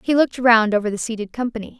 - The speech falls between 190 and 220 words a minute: No, fast, 235 wpm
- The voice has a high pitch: Yes, high, 230 Hz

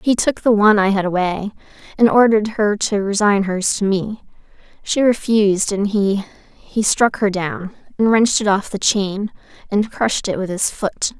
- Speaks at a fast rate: No, average, 180 wpm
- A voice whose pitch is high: Yes, high, 205 Hz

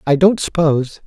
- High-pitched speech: No, medium, 155 Hz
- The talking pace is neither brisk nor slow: Yes, average, 170 wpm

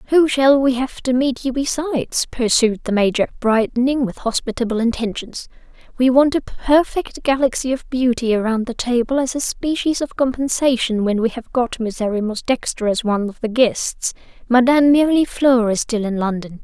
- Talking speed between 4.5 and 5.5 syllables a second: Yes, 5.0 syllables/s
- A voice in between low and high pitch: No, high, 245 Hz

